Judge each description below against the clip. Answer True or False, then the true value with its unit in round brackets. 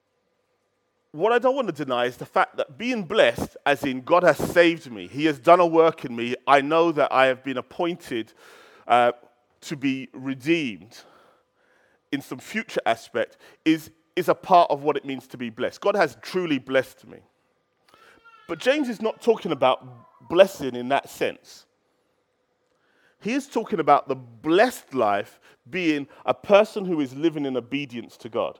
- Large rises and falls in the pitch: True (7.0 semitones)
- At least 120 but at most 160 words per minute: False (175 wpm)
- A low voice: False (160 Hz)